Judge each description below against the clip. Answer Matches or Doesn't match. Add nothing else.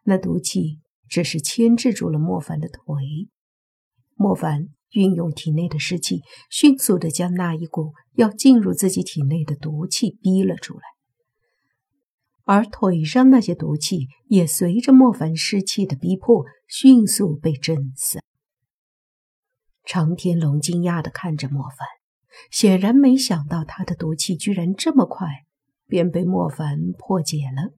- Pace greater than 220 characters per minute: Doesn't match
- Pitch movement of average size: Matches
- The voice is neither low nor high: Matches